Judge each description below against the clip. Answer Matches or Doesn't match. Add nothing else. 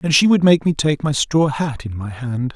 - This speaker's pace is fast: Matches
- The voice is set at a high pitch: Doesn't match